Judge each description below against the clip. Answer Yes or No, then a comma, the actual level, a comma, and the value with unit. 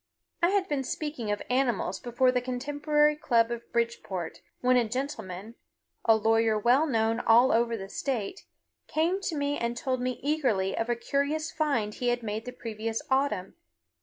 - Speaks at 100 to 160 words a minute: No, average, 170 wpm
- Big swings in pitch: No, average, 4.1 semitones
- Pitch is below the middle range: No, high, 245 Hz